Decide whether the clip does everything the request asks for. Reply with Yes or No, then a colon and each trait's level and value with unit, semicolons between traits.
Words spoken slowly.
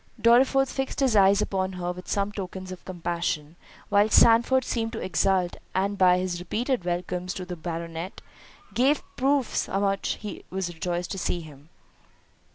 No: average, 165 wpm